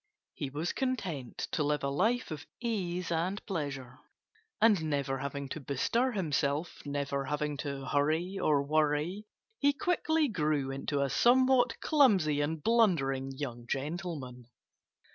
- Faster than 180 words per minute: No, slow, 135 wpm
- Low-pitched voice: No, medium, 155 Hz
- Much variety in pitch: Yes, wide, 6.2 semitones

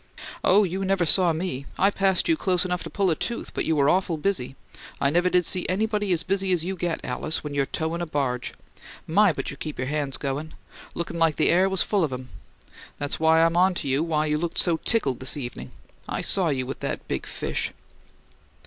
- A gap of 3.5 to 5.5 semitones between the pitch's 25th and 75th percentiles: Yes, average, 4.4 semitones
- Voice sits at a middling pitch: Yes, medium, 165 Hz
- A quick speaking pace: Yes, fast, 220 wpm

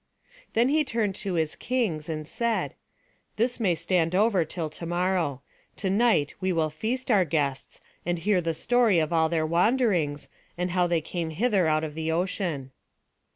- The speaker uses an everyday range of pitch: Yes, average, 4.9 semitones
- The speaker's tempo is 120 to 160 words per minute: No, average, 175 wpm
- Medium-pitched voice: Yes, medium, 175 Hz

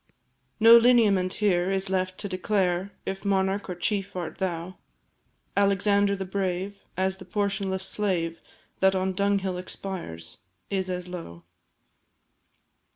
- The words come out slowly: Yes, slow, 125 wpm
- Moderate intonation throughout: No, narrow, 1.5 semitones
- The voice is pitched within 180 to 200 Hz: Yes, high, 190 Hz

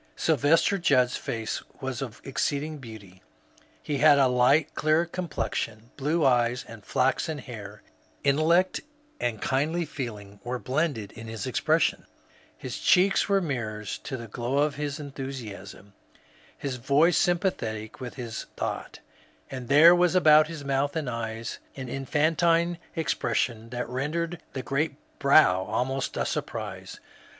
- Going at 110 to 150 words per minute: Yes, average, 140 wpm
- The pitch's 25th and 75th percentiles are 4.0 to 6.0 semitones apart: Yes, average, 4.9 semitones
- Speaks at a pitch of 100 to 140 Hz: Yes, low, 135 Hz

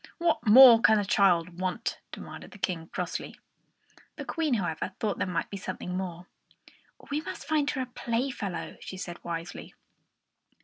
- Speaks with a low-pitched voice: No, high, 195 Hz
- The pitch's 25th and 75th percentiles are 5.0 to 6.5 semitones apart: Yes, wide, 5.4 semitones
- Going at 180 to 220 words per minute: No, average, 160 wpm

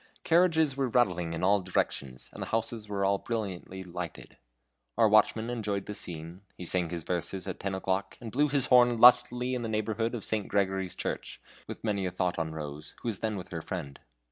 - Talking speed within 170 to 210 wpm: Yes, average, 200 wpm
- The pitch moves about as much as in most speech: Yes, average, 4.4 semitones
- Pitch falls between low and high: No, low, 100 Hz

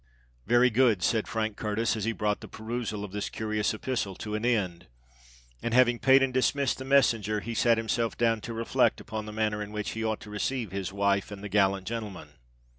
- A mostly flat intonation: Yes, narrow, 2.2 semitones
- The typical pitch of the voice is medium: No, low, 110 Hz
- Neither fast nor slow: No, fast, 210 wpm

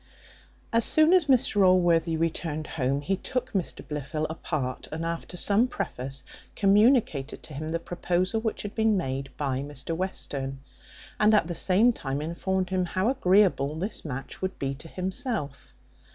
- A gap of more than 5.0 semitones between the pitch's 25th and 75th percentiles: Yes, wide, 5.6 semitones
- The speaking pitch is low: No, medium, 175 Hz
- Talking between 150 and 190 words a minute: Yes, average, 160 wpm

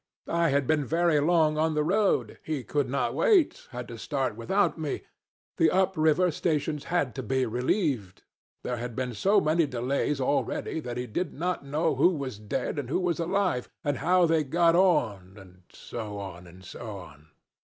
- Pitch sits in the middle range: Yes, medium, 145 Hz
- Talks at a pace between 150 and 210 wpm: Yes, average, 185 wpm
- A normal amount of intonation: No, wide, 5.7 semitones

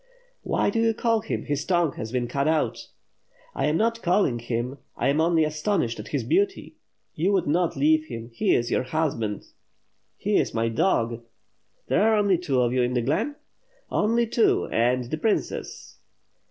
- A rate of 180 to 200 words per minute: Yes, average, 185 wpm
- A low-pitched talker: No, medium, 155 Hz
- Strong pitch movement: Yes, wide, 8.4 semitones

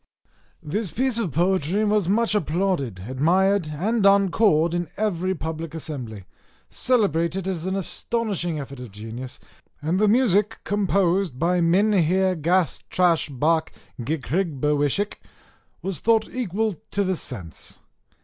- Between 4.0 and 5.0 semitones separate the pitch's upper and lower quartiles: Yes, average, 4.7 semitones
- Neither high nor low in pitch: Yes, medium, 180 Hz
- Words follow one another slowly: Yes, slow, 115 wpm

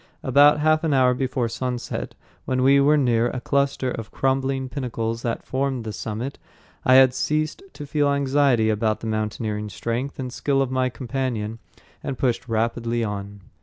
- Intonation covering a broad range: No, average, 3.2 semitones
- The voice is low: Yes, low, 130 Hz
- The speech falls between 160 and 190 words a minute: Yes, average, 165 wpm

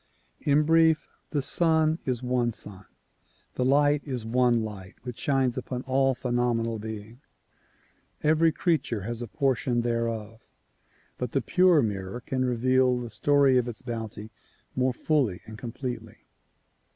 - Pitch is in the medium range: No, low, 125 Hz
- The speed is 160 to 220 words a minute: No, average, 140 wpm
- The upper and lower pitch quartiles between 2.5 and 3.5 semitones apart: Yes, average, 3.2 semitones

